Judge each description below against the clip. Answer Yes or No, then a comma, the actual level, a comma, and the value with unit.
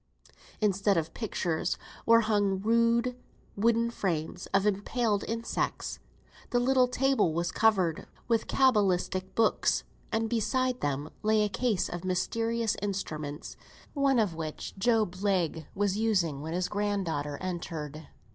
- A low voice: No, high, 205 Hz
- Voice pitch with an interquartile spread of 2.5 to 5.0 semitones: Yes, average, 4.7 semitones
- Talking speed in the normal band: No, slow, 130 wpm